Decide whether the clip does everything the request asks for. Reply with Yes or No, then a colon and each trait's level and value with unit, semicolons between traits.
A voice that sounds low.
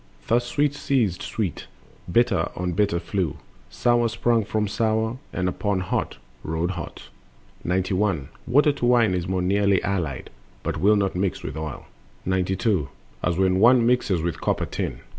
Yes: low, 100 Hz